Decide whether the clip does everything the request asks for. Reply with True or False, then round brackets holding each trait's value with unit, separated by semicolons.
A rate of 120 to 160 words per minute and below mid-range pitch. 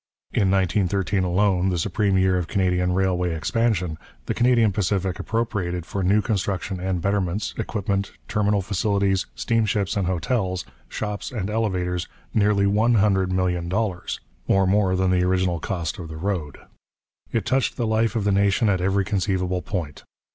True (155 wpm; 95 Hz)